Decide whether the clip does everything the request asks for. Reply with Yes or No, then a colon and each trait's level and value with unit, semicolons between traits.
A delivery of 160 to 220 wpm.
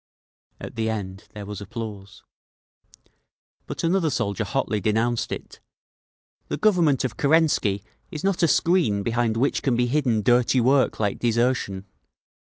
No: average, 140 wpm